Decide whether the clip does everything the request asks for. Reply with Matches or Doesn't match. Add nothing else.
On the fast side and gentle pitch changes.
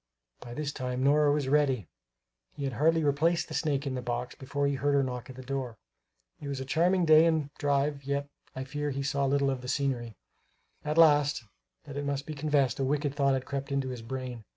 Matches